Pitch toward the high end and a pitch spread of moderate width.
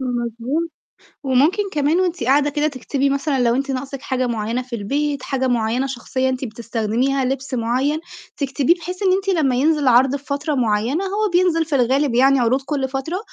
Yes: very high, 270 Hz; average, 3.0 semitones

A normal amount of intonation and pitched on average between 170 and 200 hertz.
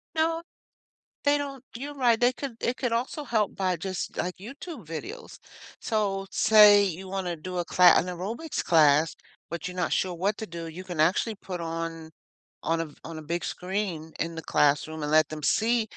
No: wide, 5.7 semitones; medium, 185 Hz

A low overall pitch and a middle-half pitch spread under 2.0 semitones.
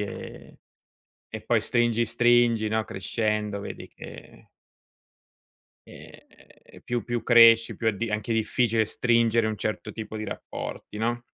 Yes: low, 115 Hz; narrow, 1.6 semitones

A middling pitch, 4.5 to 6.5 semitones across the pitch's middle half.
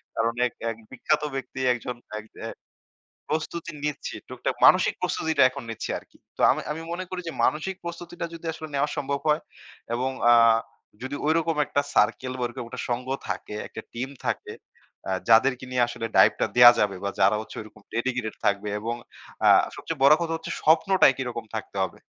No: low, 130 Hz; average, 5.1 semitones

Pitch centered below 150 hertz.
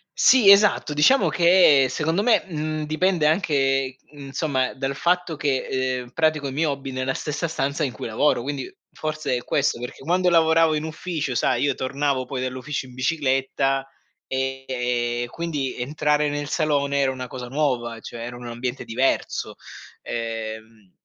Yes: medium, 140 Hz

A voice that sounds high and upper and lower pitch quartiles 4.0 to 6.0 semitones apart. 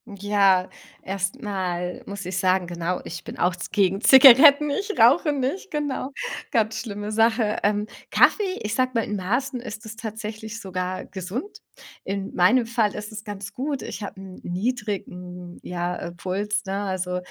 Yes: high, 205 Hz; average, 4.4 semitones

